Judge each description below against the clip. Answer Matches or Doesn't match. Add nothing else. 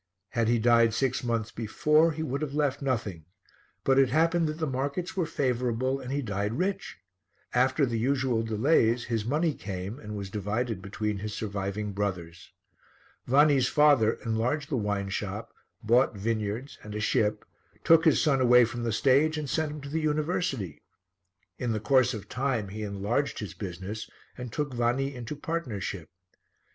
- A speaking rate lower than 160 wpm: Doesn't match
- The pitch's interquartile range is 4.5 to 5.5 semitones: Matches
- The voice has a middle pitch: Doesn't match